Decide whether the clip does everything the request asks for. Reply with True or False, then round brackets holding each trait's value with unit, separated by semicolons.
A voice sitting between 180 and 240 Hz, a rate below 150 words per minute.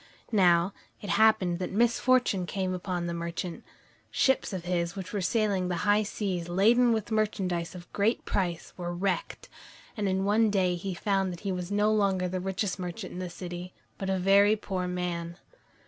False (190 Hz; 180 wpm)